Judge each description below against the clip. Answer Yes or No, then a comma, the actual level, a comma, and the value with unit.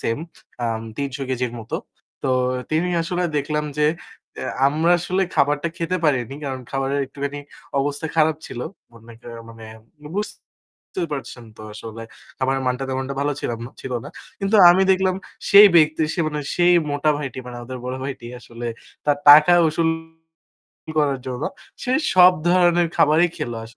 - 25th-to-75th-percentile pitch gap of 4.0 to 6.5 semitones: Yes, average, 4.4 semitones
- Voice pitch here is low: No, medium, 145 Hz